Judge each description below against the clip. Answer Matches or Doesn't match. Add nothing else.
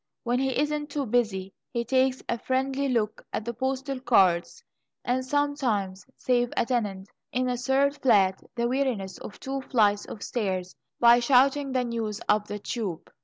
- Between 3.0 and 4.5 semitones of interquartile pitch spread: Matches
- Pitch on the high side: Matches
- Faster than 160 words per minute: Matches